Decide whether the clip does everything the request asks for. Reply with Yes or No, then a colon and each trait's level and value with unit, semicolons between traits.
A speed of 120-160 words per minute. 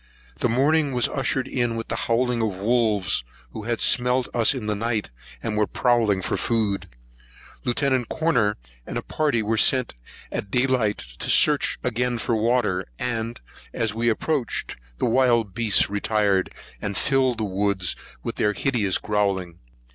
Yes: average, 155 wpm